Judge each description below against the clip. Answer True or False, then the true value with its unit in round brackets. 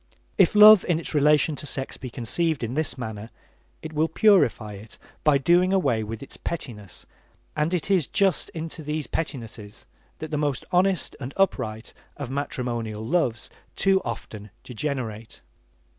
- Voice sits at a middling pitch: True (145 Hz)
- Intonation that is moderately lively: False (6.4 semitones)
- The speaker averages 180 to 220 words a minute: False (155 wpm)